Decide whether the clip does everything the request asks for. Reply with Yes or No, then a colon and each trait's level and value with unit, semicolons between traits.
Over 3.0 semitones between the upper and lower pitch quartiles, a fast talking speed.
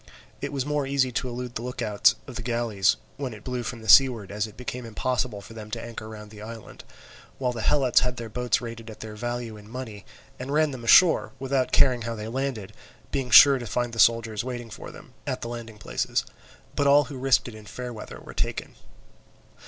No: average, 2.7 semitones; fast, 225 wpm